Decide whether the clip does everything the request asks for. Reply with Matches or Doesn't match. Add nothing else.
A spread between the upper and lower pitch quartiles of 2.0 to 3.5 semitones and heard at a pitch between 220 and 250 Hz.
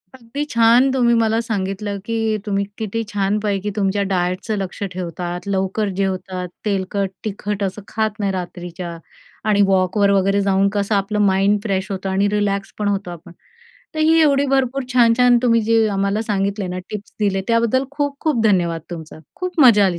Doesn't match